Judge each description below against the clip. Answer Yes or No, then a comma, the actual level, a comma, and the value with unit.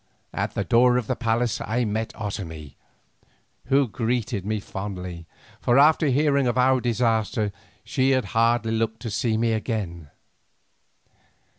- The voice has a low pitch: Yes, low, 115 Hz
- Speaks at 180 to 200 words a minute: No, average, 140 wpm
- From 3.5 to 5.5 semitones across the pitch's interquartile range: No, average, 3.0 semitones